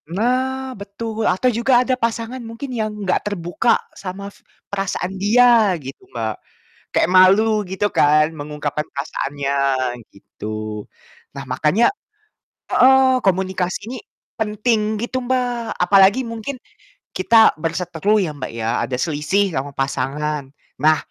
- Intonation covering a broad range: Yes, wide, 7.1 semitones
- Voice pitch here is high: Yes, high, 200 Hz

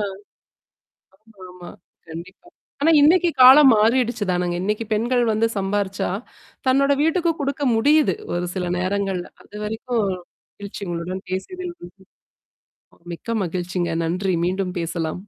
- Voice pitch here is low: No, high, 205 Hz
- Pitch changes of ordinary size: No, wide, 5.9 semitones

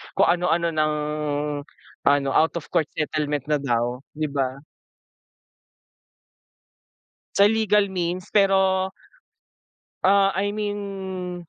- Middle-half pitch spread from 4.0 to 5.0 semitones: Yes, average, 4.5 semitones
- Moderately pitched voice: Yes, medium, 180 Hz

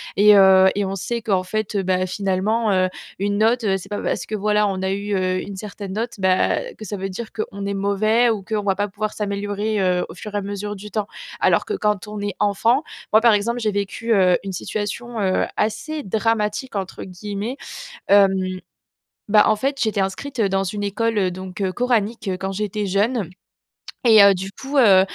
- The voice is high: Yes, high, 205 Hz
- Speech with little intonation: Yes, narrow, 2.0 semitones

